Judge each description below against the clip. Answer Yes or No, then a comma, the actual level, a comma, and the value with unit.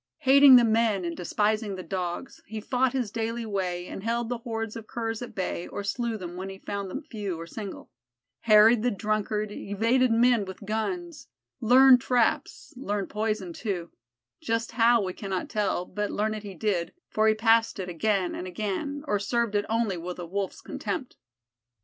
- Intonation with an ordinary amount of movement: Yes, average, 3.2 semitones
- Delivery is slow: No, average, 185 wpm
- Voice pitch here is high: Yes, high, 215 Hz